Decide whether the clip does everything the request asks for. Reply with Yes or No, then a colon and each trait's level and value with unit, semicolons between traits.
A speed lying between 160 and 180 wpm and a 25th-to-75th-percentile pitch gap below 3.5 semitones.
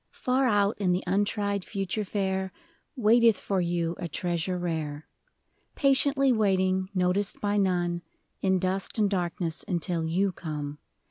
No: slow, 135 wpm; average, 2.9 semitones